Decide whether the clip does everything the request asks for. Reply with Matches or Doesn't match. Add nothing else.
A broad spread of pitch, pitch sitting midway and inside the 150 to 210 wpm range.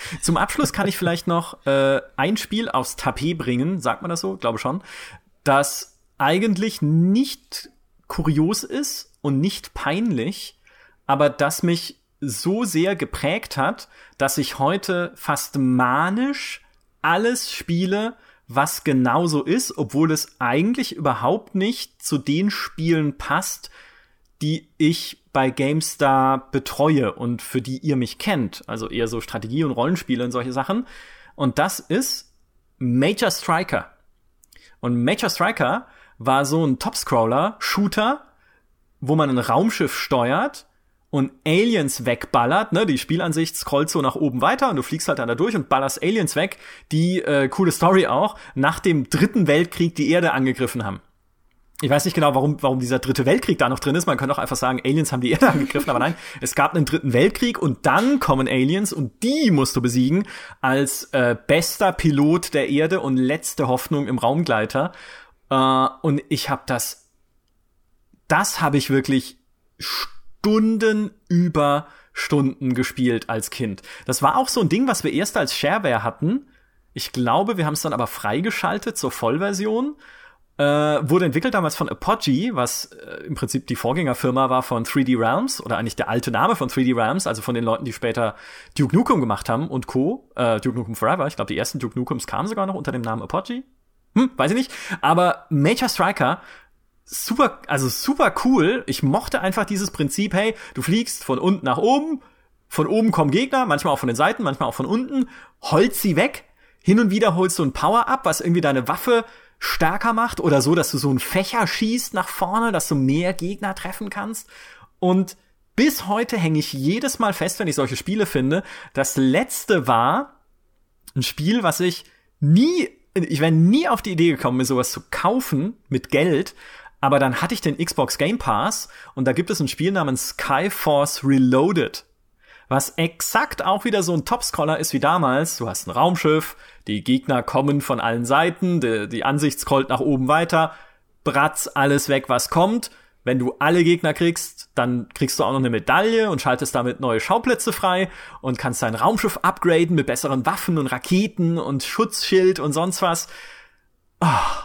Matches